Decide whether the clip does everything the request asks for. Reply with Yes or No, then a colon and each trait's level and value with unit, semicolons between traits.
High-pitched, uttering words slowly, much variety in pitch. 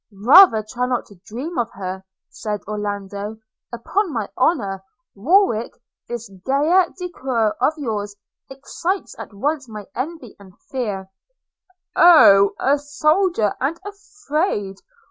Yes: high, 245 Hz; slow, 125 wpm; wide, 7.3 semitones